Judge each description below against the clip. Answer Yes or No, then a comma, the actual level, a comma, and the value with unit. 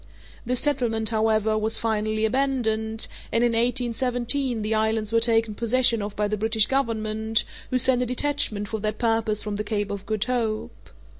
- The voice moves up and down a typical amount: No, narrow, 2.0 semitones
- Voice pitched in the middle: No, high, 225 Hz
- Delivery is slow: No, average, 170 wpm